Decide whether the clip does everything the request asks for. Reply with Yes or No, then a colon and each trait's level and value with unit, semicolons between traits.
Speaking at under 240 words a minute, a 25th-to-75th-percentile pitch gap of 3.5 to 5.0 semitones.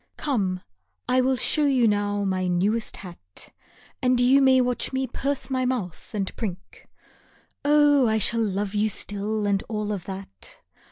Yes: average, 160 wpm; average, 4.6 semitones